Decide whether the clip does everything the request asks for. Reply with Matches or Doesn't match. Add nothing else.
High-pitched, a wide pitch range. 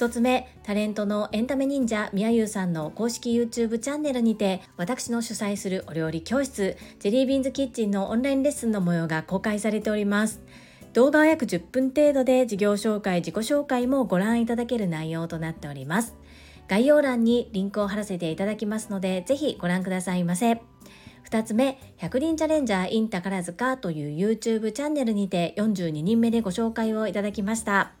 Doesn't match